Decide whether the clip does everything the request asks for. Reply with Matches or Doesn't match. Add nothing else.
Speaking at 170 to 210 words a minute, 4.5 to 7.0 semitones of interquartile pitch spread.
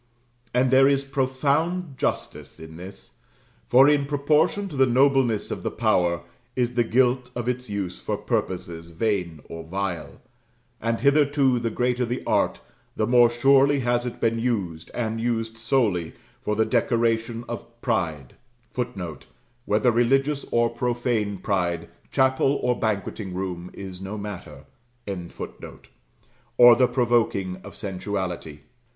Doesn't match